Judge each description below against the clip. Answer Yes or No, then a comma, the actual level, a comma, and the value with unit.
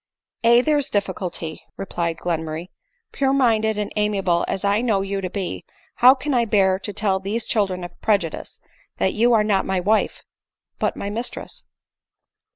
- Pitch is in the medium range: No, high, 205 Hz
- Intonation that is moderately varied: Yes, average, 3.6 semitones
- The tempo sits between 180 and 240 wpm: Yes, average, 185 wpm